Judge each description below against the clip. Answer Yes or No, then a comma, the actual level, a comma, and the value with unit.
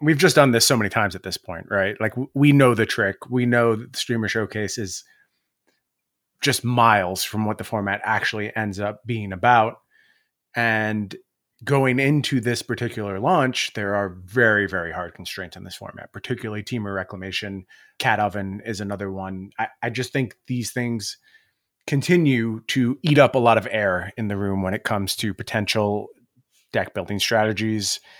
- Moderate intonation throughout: Yes, average, 3.4 semitones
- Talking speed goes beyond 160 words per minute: Yes, average, 175 wpm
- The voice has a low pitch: Yes, low, 110 Hz